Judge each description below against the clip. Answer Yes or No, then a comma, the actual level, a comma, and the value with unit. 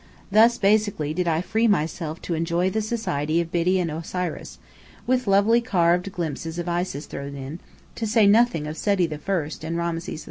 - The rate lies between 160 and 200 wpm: Yes, average, 180 wpm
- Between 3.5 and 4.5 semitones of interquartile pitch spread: Yes, average, 4.1 semitones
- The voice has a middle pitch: Yes, medium, 175 Hz